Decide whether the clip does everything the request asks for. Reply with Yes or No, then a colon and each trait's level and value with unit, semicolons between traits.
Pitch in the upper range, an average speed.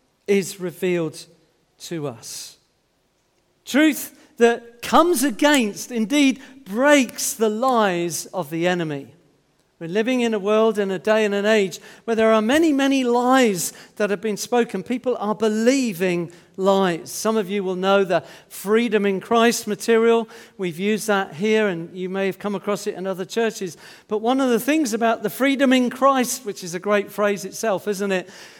Yes: high, 210 Hz; average, 180 wpm